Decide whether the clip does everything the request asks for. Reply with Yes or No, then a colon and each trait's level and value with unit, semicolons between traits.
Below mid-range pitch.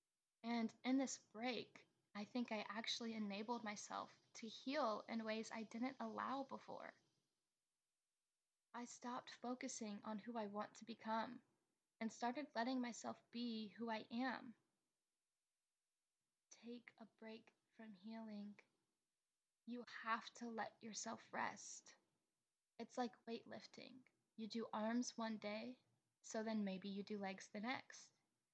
No: high, 225 Hz